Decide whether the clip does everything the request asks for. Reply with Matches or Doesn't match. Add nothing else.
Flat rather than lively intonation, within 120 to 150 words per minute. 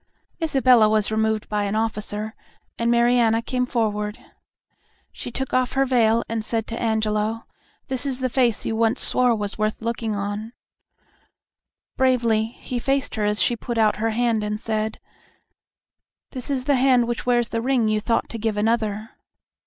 Doesn't match